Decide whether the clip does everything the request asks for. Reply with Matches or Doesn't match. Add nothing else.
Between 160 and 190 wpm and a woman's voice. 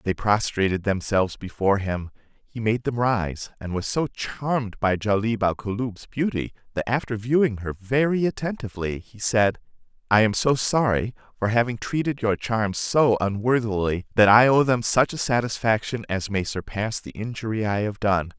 Doesn't match